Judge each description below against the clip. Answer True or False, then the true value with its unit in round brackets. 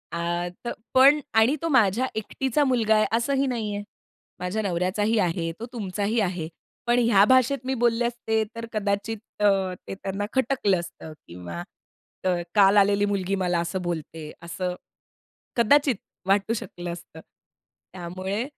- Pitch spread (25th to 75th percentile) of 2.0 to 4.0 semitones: False (4.5 semitones)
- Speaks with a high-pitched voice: True (205 Hz)